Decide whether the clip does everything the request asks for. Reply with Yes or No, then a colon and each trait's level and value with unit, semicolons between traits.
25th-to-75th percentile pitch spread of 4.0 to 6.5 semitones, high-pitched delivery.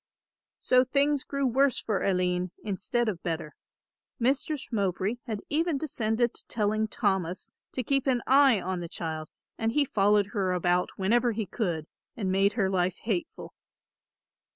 Yes: average, 5.2 semitones; high, 215 Hz